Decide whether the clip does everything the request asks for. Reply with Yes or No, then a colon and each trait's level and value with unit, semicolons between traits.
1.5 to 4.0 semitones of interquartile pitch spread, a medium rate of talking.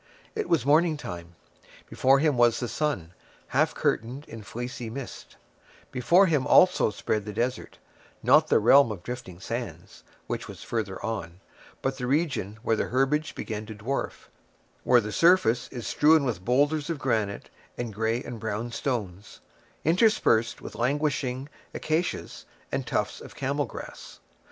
No: average, 4.9 semitones; average, 150 wpm